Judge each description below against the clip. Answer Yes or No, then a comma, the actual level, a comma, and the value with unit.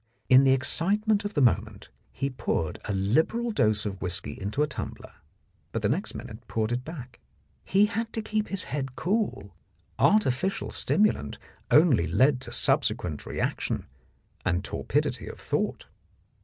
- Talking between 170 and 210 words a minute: No, average, 150 wpm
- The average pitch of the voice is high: No, low, 130 Hz